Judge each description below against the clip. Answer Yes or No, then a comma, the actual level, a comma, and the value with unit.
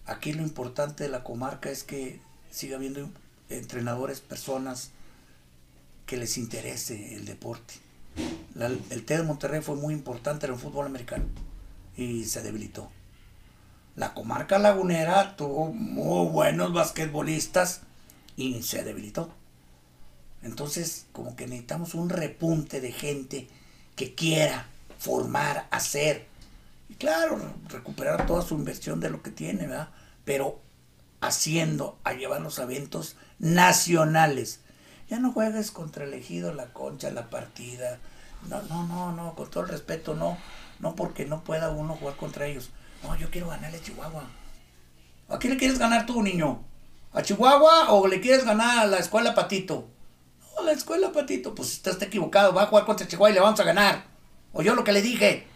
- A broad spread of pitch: Yes, wide, 7.7 semitones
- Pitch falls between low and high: Yes, medium, 145 Hz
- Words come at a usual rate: Yes, average, 155 wpm